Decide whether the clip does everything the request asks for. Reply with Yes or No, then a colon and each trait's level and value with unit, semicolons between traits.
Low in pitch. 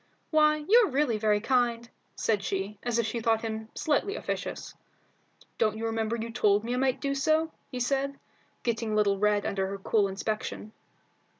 No: high, 230 Hz